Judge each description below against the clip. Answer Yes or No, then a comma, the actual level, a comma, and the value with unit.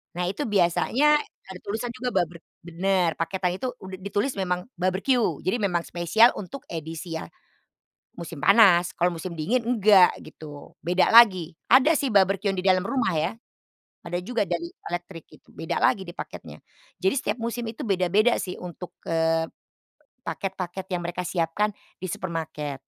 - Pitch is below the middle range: No, medium, 185 Hz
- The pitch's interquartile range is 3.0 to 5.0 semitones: Yes, average, 3.6 semitones